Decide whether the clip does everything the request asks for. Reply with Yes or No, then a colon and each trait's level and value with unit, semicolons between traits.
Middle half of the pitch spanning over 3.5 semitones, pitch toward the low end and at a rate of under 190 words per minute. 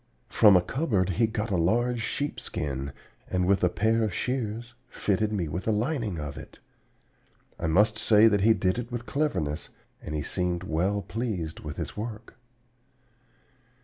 Yes: average, 4.4 semitones; low, 105 Hz; average, 165 wpm